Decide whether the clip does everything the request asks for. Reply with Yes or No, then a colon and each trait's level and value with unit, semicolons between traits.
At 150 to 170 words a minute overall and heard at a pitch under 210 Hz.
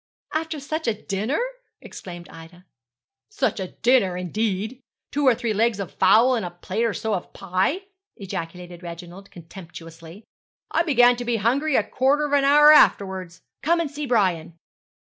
No: average, 160 wpm; high, 215 Hz